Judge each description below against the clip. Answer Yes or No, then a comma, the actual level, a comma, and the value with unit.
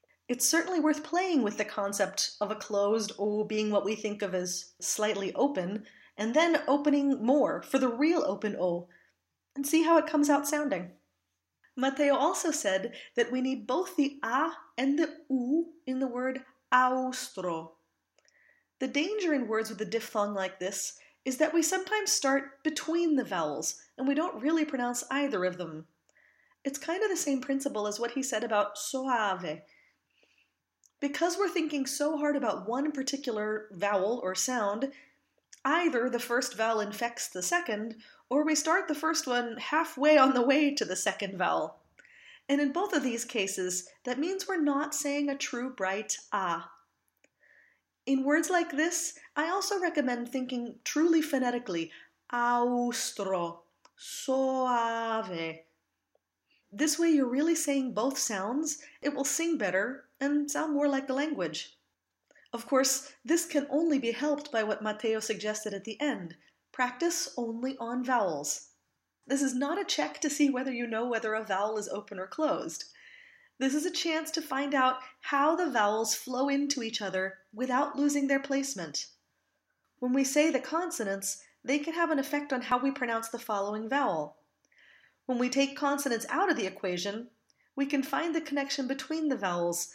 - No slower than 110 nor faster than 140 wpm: No, average, 165 wpm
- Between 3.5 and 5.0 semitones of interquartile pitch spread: No, wide, 5.4 semitones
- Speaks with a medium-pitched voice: No, very high, 265 Hz